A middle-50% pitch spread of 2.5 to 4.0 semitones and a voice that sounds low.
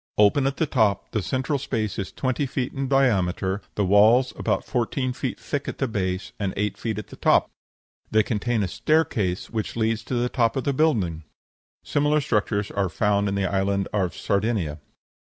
No: average, 4.6 semitones; low, 110 Hz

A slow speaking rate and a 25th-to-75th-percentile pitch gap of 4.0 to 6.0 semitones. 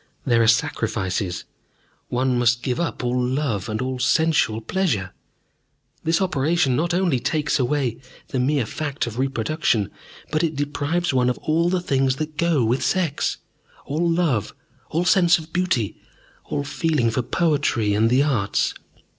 No: average, 150 wpm; average, 5.0 semitones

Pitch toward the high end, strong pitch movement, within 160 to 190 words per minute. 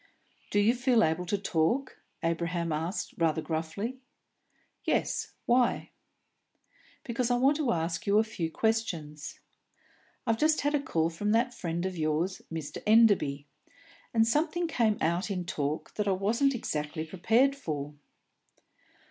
No: high, 195 Hz; wide, 6.4 semitones; average, 140 wpm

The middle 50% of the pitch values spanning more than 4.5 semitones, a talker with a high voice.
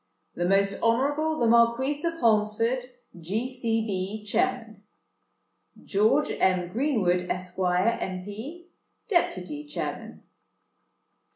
Yes: average, 5.3 semitones; high, 225 Hz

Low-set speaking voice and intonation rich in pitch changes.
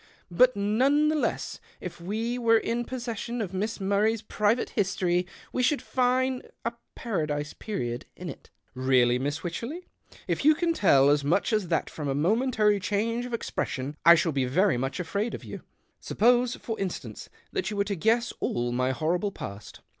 No: high, 205 Hz; wide, 7.1 semitones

